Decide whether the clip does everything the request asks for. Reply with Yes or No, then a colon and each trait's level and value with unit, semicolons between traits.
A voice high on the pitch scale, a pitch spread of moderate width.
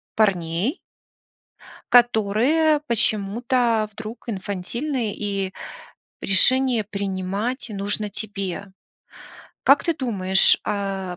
Yes: high, 210 Hz; average, 3.6 semitones